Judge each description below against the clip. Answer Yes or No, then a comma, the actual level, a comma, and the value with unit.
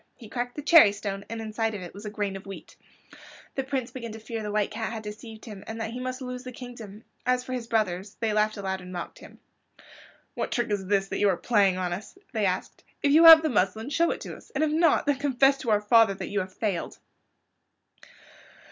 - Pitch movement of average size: Yes, average, 3.9 semitones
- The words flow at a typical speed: No, fast, 245 wpm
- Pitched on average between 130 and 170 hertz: No, high, 220 Hz